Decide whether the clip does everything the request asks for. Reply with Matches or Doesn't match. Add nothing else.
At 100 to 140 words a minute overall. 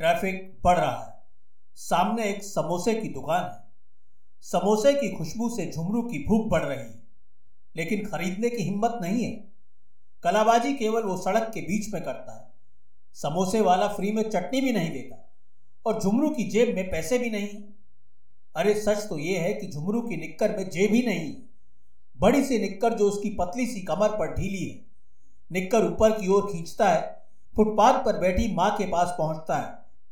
Doesn't match